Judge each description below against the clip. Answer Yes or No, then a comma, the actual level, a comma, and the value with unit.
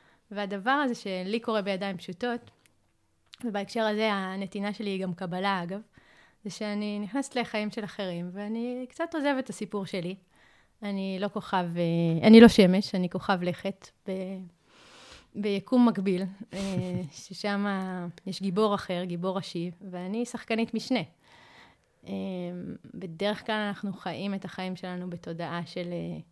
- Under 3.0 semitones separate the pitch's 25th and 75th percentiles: Yes, narrow, 2.6 semitones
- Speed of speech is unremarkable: Yes, average, 125 wpm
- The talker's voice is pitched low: No, high, 195 Hz